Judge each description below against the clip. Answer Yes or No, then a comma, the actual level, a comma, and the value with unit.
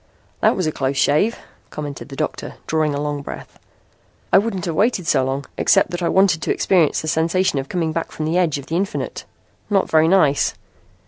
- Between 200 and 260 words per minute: Yes, fast, 205 wpm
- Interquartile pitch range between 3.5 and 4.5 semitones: Yes, average, 4.0 semitones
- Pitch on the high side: No, medium, 160 Hz